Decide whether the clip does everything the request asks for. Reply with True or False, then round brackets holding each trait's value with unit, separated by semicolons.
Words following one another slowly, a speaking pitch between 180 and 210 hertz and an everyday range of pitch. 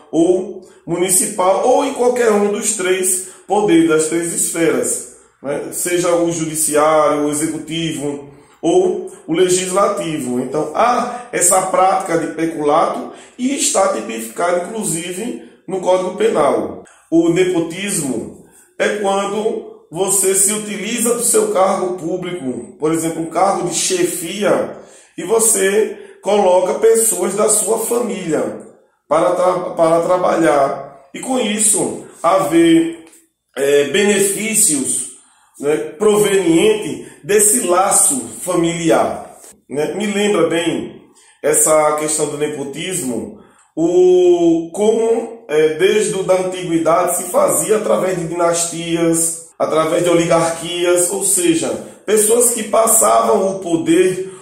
False (110 wpm; 185 Hz; 6.1 semitones)